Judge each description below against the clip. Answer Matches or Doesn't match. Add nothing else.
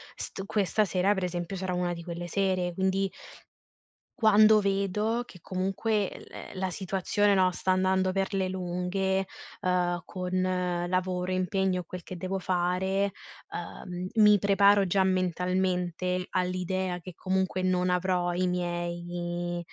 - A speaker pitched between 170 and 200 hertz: Matches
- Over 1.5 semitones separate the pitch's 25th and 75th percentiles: Doesn't match